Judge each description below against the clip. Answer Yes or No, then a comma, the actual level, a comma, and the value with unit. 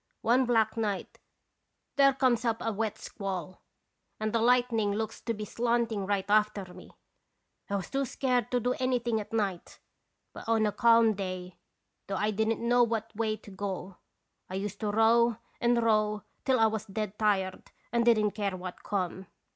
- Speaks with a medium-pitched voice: No, high, 220 Hz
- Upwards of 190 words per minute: No, average, 175 wpm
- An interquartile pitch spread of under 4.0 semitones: Yes, narrow, 2.6 semitones